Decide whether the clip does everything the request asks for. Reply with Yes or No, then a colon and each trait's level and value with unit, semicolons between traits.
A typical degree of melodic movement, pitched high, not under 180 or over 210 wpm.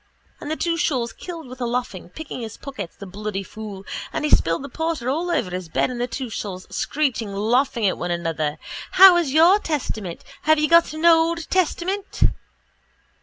No: wide, 8.2 semitones; very high, 255 Hz; average, 190 wpm